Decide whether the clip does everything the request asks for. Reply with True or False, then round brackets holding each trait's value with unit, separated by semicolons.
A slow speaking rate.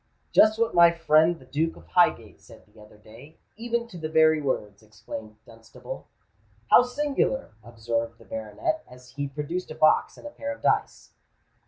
False (170 wpm)